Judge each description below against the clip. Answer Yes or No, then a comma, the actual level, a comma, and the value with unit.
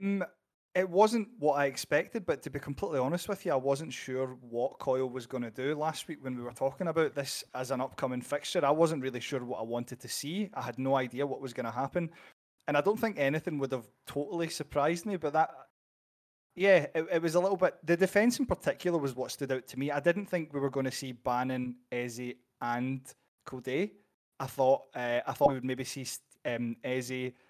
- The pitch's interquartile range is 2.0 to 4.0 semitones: No, average, 4.5 semitones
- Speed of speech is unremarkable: No, fast, 225 wpm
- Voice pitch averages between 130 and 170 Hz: Yes, low, 135 Hz